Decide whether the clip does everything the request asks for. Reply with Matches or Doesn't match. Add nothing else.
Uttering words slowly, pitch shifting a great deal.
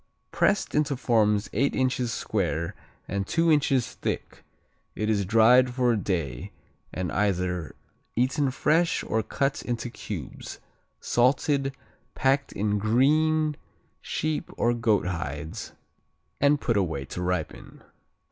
Matches